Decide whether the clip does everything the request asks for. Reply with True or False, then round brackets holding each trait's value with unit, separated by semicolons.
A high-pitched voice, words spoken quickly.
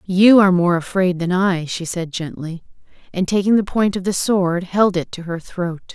False (180 Hz; 210 wpm)